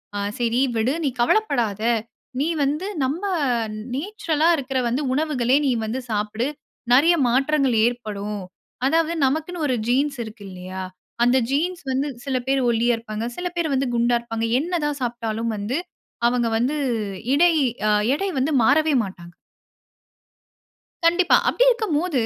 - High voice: Yes, very high, 260 Hz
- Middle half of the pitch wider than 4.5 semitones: Yes, average, 4.9 semitones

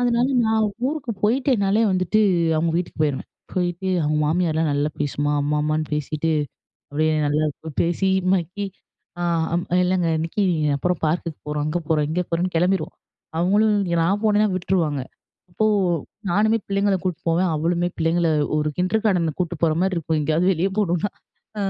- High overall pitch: No, medium, 175 Hz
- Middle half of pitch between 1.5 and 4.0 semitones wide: Yes, average, 3.7 semitones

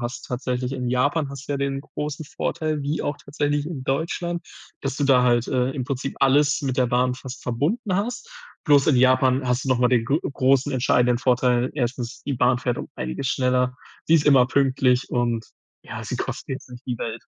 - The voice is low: Yes, low, 130 Hz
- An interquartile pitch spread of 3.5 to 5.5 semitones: No, narrow, 2.5 semitones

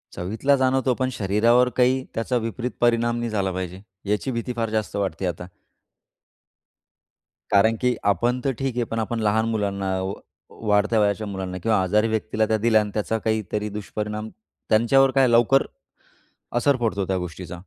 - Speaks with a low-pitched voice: Yes, low, 110 Hz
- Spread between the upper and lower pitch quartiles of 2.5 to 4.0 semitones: Yes, average, 2.9 semitones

